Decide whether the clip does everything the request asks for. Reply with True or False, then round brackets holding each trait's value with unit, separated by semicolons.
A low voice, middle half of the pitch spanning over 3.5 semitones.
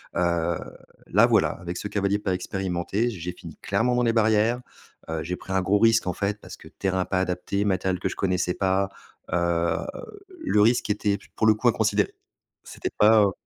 False (100 Hz; 2.7 semitones)